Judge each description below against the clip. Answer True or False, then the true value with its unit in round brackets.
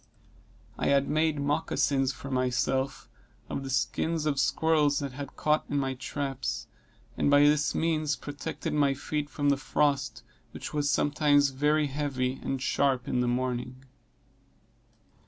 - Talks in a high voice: False (140 Hz)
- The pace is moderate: True (150 wpm)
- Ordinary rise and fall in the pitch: False (1.9 semitones)